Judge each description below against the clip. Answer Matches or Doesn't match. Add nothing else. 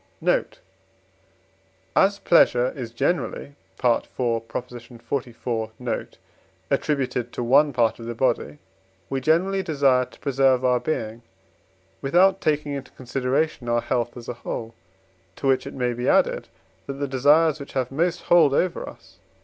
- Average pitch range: Matches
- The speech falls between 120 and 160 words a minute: Matches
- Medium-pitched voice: Doesn't match